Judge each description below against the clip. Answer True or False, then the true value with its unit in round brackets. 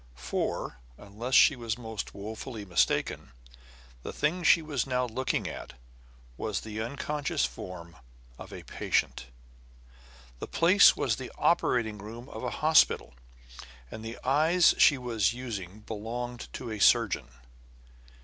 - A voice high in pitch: False (115 Hz)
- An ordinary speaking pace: False (130 wpm)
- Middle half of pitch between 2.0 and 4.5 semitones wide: True (4.0 semitones)